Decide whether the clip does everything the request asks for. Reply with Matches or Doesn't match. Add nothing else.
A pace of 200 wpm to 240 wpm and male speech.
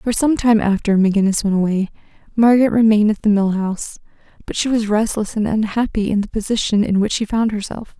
Doesn't match